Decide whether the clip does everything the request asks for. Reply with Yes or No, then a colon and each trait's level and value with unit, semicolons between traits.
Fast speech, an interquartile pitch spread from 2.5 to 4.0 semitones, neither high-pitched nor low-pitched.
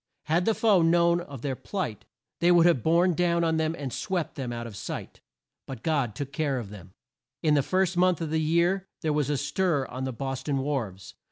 No: fast, 225 wpm; average, 4.5 semitones; medium, 155 Hz